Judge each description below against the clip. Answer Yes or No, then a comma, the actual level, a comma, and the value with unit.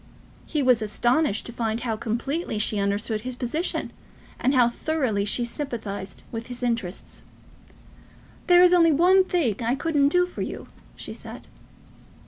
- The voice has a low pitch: No, high, 245 Hz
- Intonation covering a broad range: Yes, wide, 6.0 semitones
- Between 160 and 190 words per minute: No, average, 150 wpm